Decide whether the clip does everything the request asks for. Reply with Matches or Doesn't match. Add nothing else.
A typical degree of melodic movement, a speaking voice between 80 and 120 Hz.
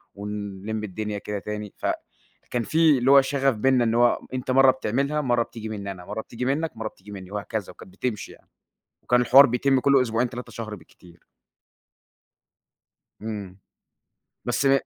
Matches